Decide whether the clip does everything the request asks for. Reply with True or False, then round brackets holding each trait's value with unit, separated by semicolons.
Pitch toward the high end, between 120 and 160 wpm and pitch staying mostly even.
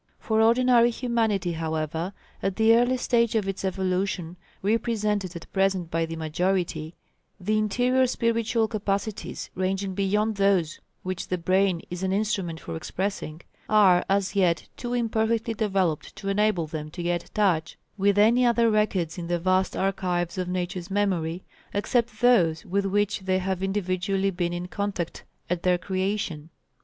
False (195 Hz; 150 wpm; 3.3 semitones)